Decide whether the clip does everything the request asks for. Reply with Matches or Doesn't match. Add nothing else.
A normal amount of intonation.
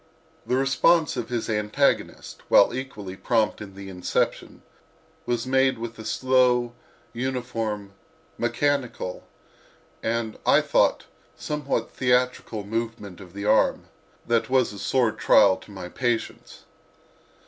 Matches